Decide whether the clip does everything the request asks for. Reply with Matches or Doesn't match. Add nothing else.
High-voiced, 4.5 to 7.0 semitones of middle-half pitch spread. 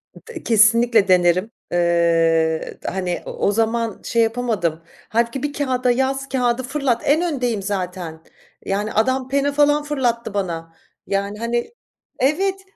Matches